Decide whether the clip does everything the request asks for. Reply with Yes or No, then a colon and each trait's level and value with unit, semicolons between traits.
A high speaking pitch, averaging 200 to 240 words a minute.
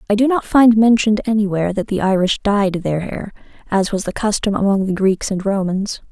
Yes: high, 200 Hz; fast, 205 wpm